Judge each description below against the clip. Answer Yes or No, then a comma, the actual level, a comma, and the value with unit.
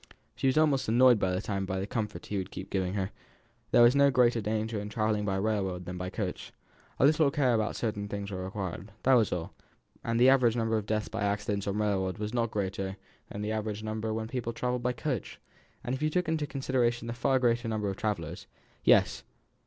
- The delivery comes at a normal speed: No, fast, 215 wpm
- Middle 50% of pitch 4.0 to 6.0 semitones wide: No, average, 3.5 semitones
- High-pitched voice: No, low, 110 Hz